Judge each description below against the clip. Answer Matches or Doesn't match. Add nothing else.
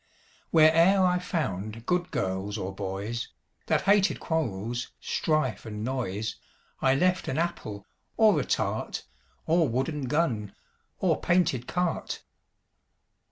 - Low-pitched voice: Matches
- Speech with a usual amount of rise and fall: Doesn't match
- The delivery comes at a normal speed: Doesn't match